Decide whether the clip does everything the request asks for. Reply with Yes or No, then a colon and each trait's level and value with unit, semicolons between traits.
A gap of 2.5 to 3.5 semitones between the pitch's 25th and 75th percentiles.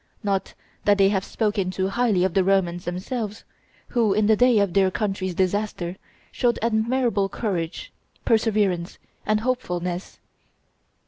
Yes: average, 2.8 semitones